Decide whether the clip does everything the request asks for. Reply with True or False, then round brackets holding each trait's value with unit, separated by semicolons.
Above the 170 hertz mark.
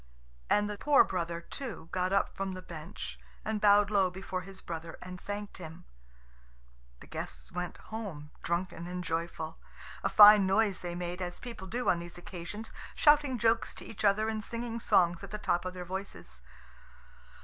True (190 Hz)